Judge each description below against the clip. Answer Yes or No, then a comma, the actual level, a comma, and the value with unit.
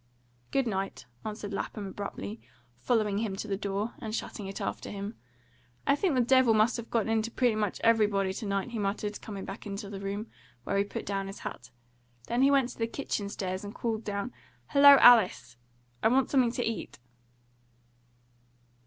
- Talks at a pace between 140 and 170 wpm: No, average, 185 wpm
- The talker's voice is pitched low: No, high, 210 Hz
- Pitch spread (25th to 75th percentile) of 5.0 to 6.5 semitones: No, average, 3.0 semitones